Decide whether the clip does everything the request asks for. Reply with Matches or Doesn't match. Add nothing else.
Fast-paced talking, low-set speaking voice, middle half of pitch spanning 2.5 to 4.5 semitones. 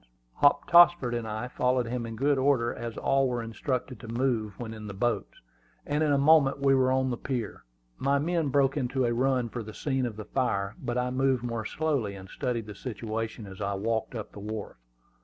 Matches